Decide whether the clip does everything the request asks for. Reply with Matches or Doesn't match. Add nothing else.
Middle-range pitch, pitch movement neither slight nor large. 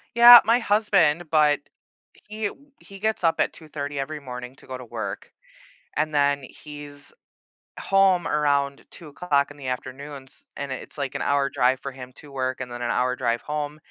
Matches